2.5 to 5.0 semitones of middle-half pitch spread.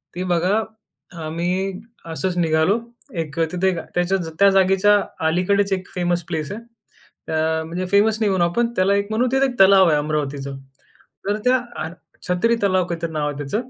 Yes: average, 3.7 semitones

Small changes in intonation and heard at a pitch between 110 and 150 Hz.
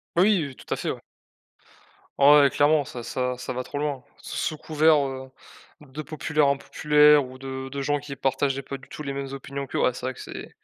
Yes: narrow, 2.0 semitones; medium, 140 Hz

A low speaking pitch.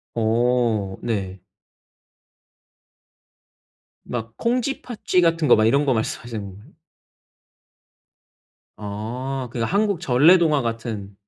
Yes: low, 120 Hz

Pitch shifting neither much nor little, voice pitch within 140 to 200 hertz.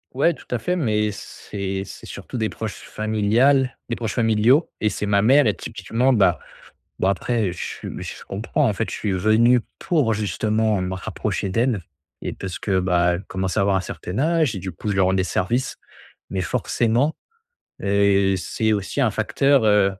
No: average, 3.7 semitones; low, 105 Hz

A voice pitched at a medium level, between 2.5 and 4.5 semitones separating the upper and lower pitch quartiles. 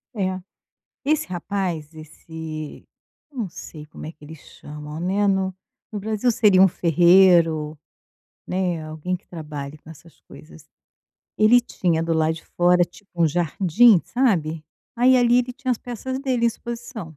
No: medium, 180 Hz; average, 5.2 semitones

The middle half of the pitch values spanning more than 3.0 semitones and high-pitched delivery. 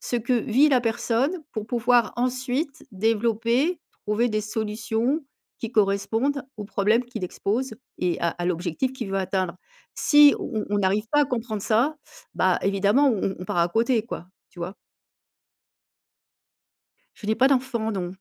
Yes: average, 4.0 semitones; high, 225 Hz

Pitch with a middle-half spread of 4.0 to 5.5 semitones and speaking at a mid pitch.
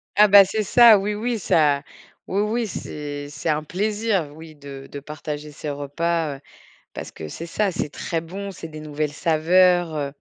Yes: average, 5.1 semitones; medium, 165 Hz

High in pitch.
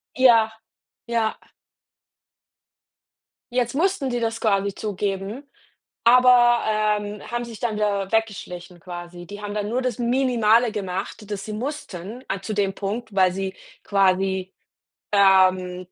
Yes: high, 210 Hz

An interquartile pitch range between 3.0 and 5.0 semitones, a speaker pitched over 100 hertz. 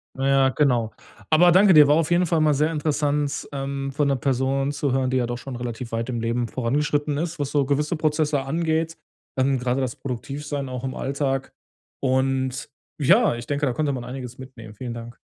No: narrow, 2.6 semitones; low, 135 Hz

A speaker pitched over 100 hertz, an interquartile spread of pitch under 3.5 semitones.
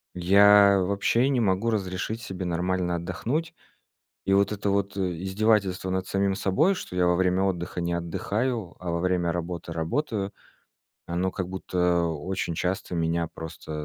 No: very low, 95 Hz; narrow, 2.4 semitones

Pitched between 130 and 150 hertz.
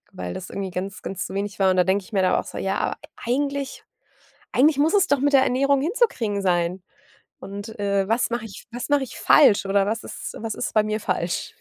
No: high, 215 Hz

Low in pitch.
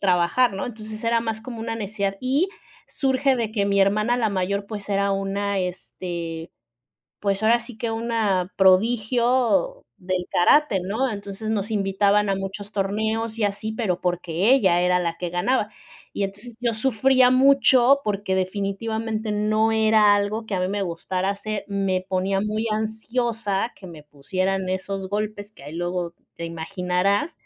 No: high, 205 Hz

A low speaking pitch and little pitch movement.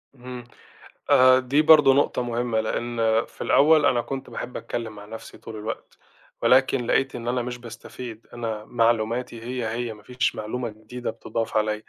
Yes: low, 120 Hz; narrow, 2.1 semitones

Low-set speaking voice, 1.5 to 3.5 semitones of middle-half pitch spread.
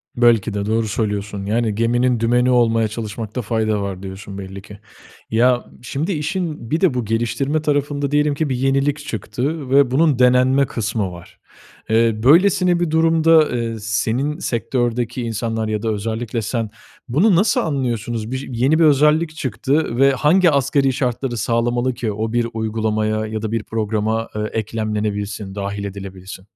No: low, 120 Hz; average, 4.2 semitones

